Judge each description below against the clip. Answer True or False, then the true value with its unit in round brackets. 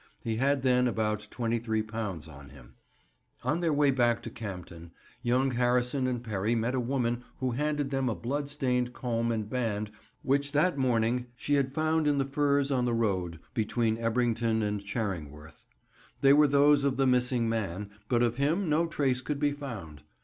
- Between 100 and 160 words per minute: False (175 wpm)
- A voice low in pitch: True (125 Hz)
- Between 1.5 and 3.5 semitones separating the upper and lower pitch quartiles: False (3.9 semitones)